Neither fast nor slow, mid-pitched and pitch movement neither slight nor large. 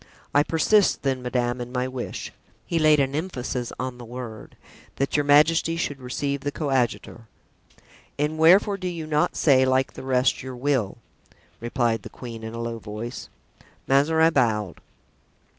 No: average, 160 wpm; low, 130 Hz; average, 3.6 semitones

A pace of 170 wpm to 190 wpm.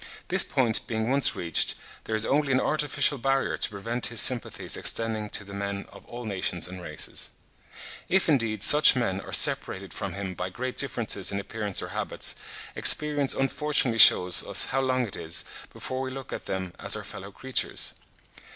Yes: average, 180 wpm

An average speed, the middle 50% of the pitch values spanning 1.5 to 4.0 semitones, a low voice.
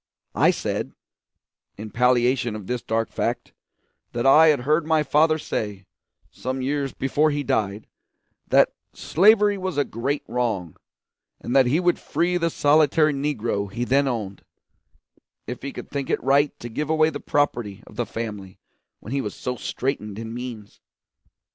No: average, 160 wpm; average, 4.9 semitones; low, 130 Hz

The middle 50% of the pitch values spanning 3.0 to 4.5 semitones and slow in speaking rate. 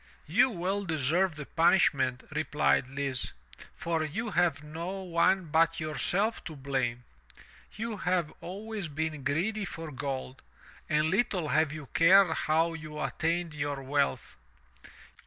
Yes: average, 4.1 semitones; slow, 130 wpm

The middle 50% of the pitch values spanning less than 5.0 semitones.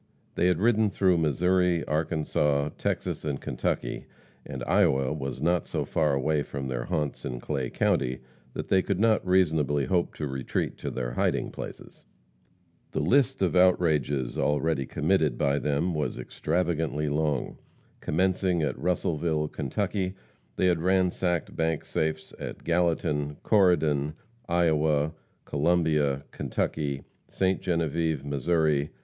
Yes: average, 3.6 semitones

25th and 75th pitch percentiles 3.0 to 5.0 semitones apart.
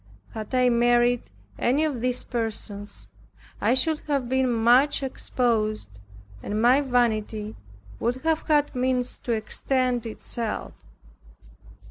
No: narrow, 2.6 semitones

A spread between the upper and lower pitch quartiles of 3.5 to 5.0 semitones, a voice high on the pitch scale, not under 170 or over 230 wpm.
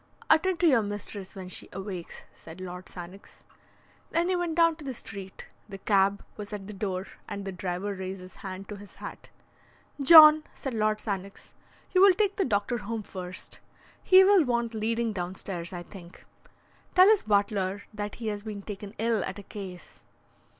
Yes: average, 4.0 semitones; high, 205 Hz; average, 180 wpm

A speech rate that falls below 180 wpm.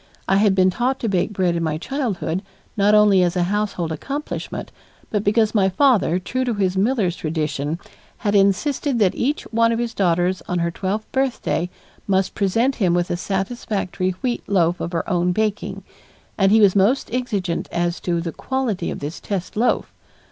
No: average, 185 wpm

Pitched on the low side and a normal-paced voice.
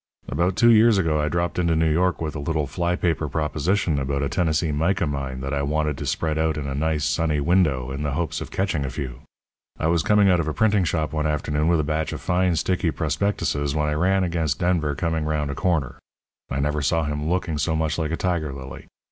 No: very low, 80 Hz; fast, 235 wpm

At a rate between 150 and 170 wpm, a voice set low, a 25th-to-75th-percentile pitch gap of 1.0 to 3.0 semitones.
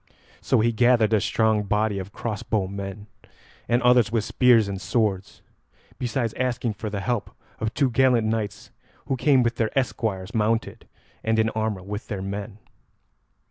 Yes: average, 160 wpm; low, 110 Hz; narrow, 2.5 semitones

